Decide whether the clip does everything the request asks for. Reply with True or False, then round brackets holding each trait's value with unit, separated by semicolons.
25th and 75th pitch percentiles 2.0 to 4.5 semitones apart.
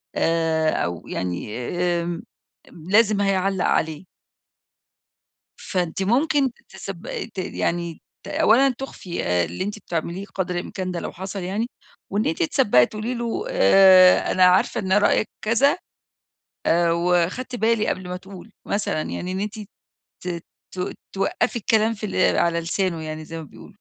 True (4.0 semitones)